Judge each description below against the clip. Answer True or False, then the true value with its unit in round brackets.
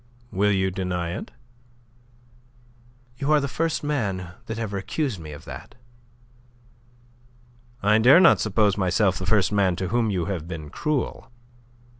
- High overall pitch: False (100 Hz)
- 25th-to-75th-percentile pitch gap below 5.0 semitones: True (4.0 semitones)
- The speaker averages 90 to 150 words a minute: True (145 wpm)